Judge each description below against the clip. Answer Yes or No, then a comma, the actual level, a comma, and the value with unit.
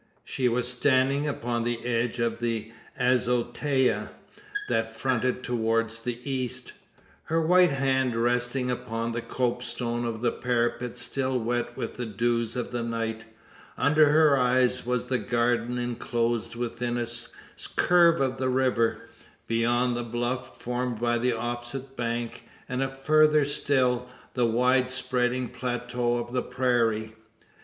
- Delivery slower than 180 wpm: Yes, slow, 135 wpm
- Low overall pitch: Yes, low, 120 Hz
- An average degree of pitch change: No, narrow, 1.5 semitones